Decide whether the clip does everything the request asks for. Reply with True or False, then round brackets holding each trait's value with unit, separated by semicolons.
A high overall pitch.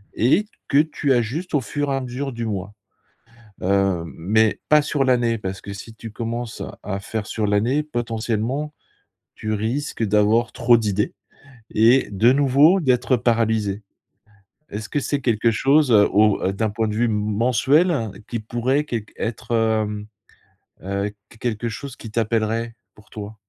False (115 Hz)